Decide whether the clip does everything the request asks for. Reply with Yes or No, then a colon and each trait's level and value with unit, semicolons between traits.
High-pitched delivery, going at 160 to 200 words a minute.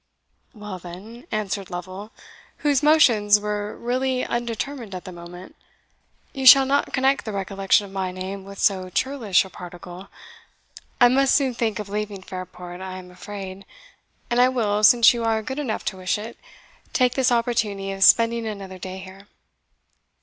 Yes: high, 210 Hz; average, 165 wpm